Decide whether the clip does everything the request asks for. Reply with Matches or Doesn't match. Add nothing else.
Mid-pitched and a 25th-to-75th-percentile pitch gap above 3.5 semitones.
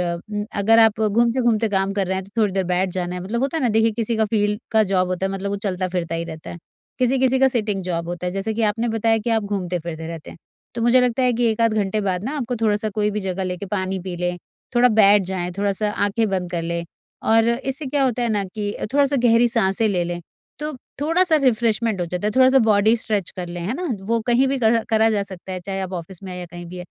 Doesn't match